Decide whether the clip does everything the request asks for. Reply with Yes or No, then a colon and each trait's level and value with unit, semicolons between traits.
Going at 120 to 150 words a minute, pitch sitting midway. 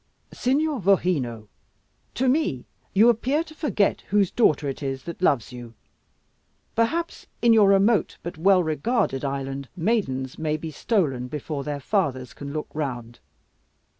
Yes: average, 140 wpm; medium, 160 Hz